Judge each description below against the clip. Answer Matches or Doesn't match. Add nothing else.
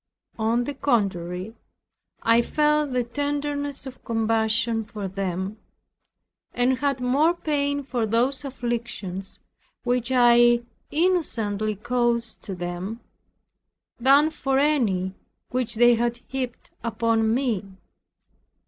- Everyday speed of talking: Doesn't match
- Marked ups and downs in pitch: Doesn't match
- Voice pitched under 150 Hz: Doesn't match